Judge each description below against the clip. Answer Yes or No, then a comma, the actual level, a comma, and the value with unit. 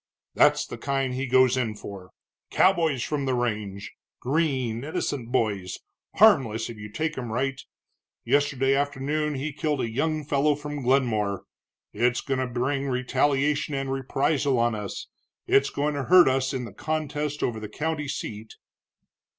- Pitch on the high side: No, low, 135 Hz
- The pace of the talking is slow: No, average, 155 wpm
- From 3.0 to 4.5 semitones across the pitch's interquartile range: Yes, average, 3.6 semitones